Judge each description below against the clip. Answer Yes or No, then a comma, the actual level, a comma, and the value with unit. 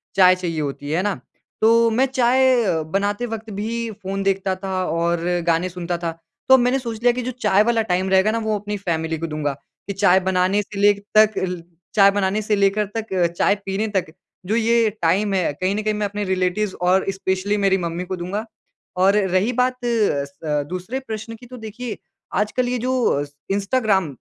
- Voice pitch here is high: Yes, high, 200 Hz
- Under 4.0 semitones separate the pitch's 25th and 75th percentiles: Yes, average, 3.4 semitones